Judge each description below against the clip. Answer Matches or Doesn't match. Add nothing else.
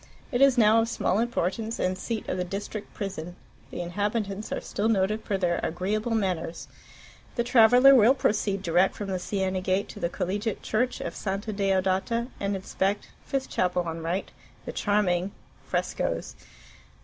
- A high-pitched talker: Matches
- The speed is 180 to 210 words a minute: Doesn't match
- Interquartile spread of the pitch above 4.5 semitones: Doesn't match